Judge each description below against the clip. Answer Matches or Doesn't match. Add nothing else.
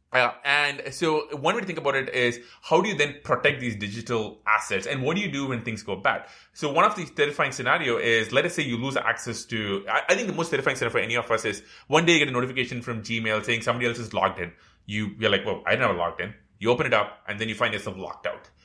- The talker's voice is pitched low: Matches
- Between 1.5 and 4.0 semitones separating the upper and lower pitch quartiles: Doesn't match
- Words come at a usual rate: Doesn't match